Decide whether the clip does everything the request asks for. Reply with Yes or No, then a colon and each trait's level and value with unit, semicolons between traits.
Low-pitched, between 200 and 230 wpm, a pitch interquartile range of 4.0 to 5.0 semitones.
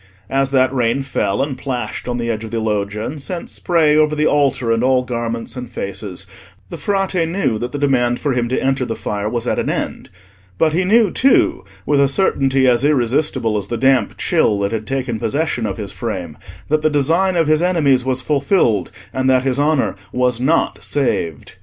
Yes: low, 130 Hz; fast, 205 wpm; average, 4.5 semitones